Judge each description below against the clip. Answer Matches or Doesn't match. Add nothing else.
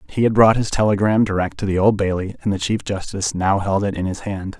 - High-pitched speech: Doesn't match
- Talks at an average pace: Doesn't match